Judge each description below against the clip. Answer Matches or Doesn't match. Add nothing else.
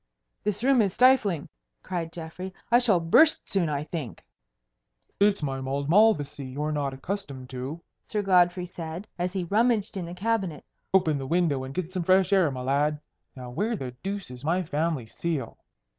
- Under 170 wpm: Doesn't match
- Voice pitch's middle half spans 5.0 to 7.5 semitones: Matches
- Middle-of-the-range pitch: Matches